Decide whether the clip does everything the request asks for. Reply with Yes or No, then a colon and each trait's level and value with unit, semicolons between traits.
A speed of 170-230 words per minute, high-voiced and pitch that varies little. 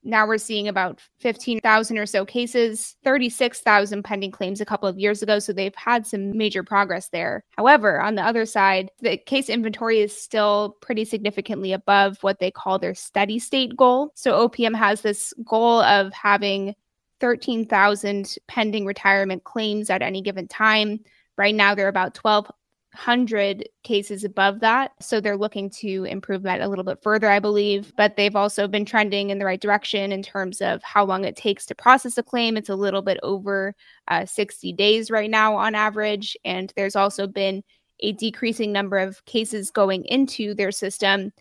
Yes: average, 180 wpm; high, 205 Hz; narrow, 2.1 semitones